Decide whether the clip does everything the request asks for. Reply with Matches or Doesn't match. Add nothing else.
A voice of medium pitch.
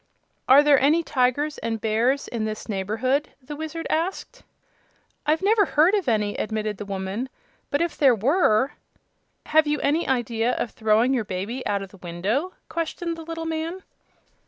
Doesn't match